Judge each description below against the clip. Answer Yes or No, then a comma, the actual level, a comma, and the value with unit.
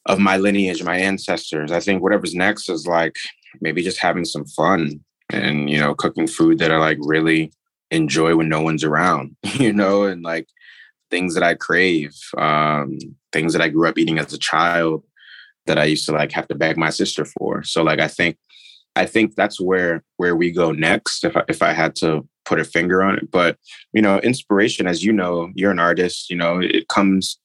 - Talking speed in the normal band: No, fast, 210 wpm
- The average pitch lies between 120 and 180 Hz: No, very low, 85 Hz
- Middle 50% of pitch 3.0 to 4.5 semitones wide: Yes, average, 3.3 semitones